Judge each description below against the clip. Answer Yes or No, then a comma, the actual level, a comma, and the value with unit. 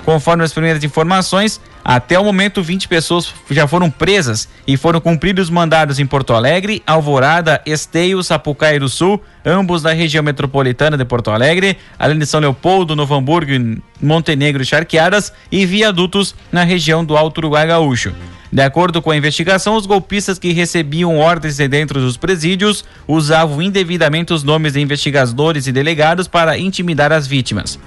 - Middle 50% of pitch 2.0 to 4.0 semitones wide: Yes, average, 3.3 semitones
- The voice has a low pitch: No, medium, 160 Hz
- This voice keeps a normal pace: Yes, average, 160 wpm